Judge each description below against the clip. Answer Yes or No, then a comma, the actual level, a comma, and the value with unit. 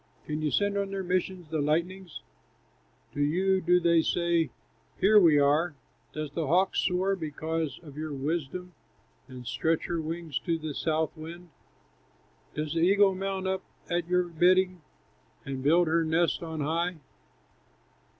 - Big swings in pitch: No, average, 2.7 semitones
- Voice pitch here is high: No, medium, 170 Hz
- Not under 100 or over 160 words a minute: Yes, average, 150 wpm